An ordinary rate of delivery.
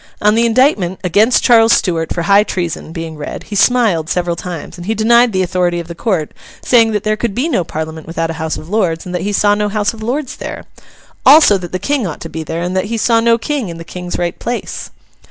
No: fast, 245 wpm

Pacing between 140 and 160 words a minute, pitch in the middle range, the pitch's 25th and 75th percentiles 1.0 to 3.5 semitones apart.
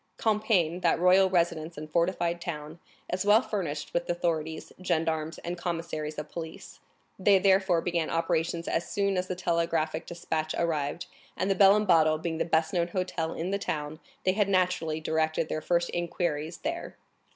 No: average, 170 wpm; medium, 170 Hz; narrow, 2.4 semitones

